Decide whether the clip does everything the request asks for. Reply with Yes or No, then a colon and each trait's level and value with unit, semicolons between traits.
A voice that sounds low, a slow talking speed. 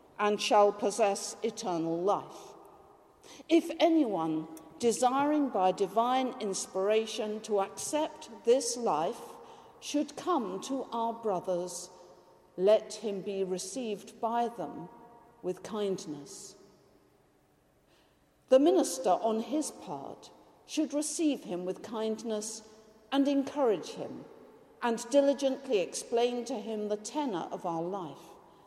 No: high, 225 Hz; slow, 105 wpm